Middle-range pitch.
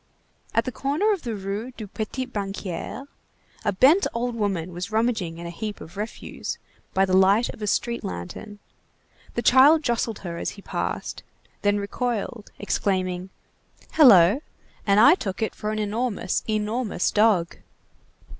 No: high, 210 Hz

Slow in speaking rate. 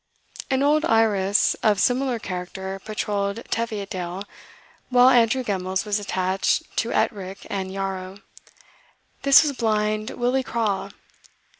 Yes: slow, 115 wpm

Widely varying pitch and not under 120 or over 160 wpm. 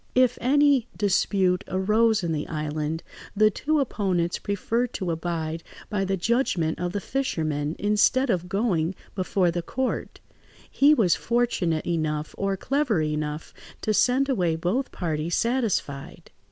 Yes: wide, 6.2 semitones; average, 140 wpm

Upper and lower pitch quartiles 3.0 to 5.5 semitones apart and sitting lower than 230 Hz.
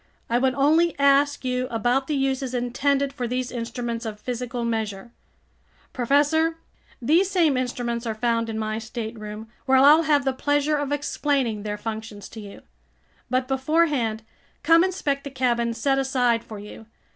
No: average, 3.6 semitones; very high, 255 Hz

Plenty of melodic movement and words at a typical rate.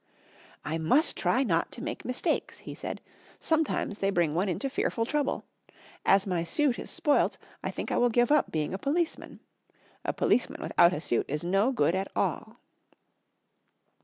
Yes: wide, 8.3 semitones; average, 170 wpm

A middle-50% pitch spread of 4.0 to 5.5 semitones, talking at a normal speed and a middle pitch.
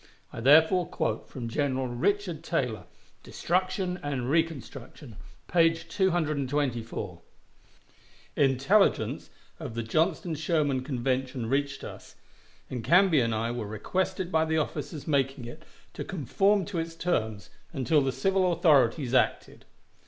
No: average, 5.1 semitones; slow, 125 wpm; medium, 145 Hz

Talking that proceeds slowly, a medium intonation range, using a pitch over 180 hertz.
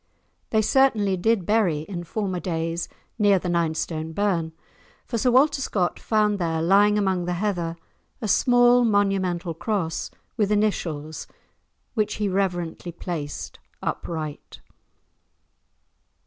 Yes: slow, 120 wpm; average, 3.8 semitones; high, 190 Hz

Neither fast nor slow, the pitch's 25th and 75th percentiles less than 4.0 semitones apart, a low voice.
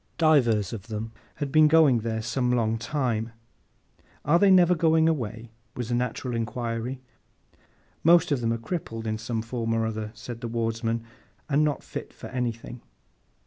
No: average, 160 wpm; average, 4.3 semitones; low, 120 Hz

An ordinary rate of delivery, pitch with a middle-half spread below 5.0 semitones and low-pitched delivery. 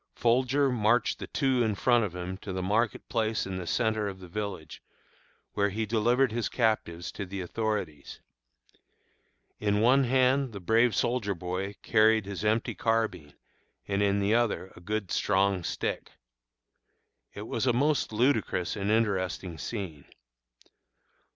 Yes: average, 150 wpm; average, 3.5 semitones; low, 105 Hz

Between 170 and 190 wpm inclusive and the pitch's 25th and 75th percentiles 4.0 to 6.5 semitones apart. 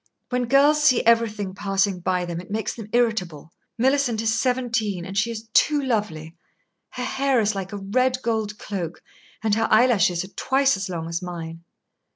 Yes: average, 180 wpm; average, 4.9 semitones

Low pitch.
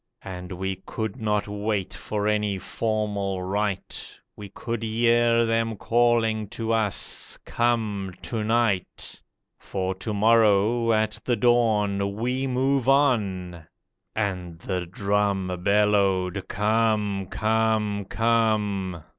Yes: low, 105 Hz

